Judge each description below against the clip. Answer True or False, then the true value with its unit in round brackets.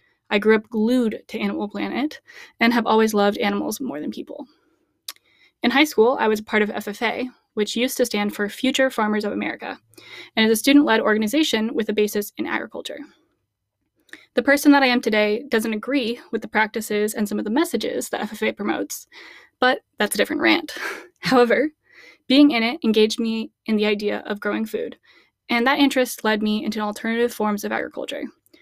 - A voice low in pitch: False (230 Hz)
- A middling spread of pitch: True (4.5 semitones)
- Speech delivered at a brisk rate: False (185 wpm)